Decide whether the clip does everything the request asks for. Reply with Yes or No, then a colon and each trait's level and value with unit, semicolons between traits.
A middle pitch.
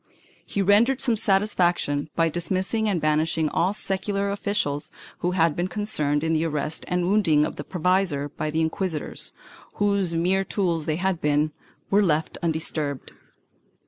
Yes: medium, 175 Hz